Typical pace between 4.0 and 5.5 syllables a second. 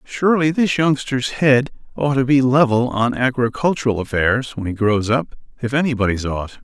Yes: 5.0 syllables/s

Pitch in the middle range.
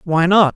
Yes: medium, 175 Hz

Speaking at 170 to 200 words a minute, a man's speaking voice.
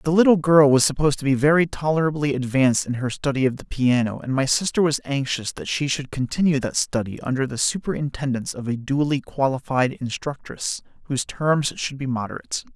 Yes: average, 190 wpm; male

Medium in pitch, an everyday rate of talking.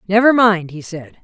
No: high, 195 Hz; average, 195 wpm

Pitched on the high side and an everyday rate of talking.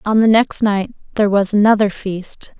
Yes: high, 205 Hz; average, 185 wpm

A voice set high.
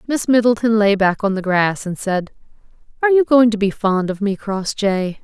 Yes: high, 210 Hz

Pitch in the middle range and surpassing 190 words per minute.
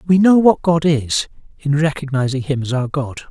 Yes: medium, 150 Hz; average, 200 wpm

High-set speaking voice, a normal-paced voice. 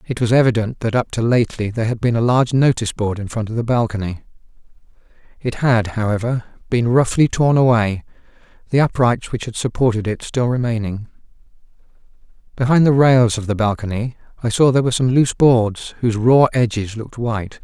No: low, 120 Hz; average, 175 wpm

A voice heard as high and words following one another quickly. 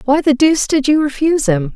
Yes: very high, 275 Hz; fast, 240 wpm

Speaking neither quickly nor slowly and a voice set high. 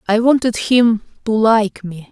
Yes: average, 170 wpm; high, 220 Hz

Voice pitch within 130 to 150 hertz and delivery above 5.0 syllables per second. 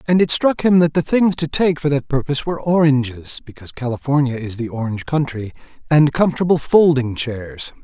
Yes: medium, 140 Hz; 5.7 syllables/s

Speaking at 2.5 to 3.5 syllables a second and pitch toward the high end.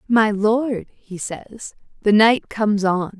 Yes: 3.3 syllables/s; high, 210 Hz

